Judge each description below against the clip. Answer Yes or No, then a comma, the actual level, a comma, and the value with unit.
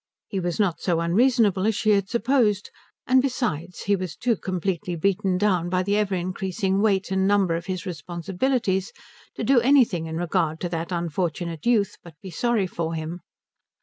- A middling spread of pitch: Yes, average, 3.4 semitones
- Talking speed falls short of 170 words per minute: No, average, 180 wpm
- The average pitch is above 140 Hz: Yes, high, 190 Hz